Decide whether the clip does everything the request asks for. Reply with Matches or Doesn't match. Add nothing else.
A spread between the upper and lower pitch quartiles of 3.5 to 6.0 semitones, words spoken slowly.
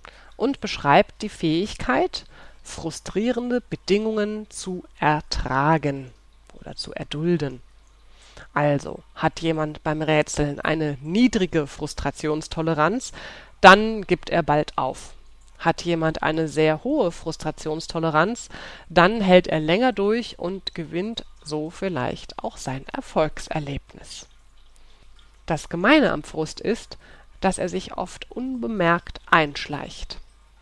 Matches